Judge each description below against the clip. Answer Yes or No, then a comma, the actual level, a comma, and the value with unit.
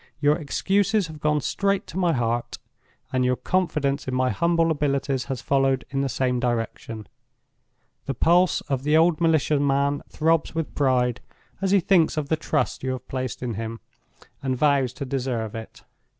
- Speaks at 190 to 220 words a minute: No, average, 175 wpm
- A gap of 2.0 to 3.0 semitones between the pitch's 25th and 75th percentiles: No, average, 4.0 semitones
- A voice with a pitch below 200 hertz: Yes, medium, 140 Hz